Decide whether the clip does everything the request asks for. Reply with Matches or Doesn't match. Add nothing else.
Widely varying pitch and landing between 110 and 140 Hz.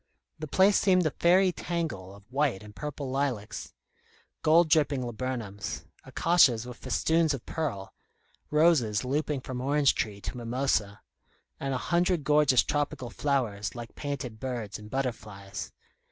Doesn't match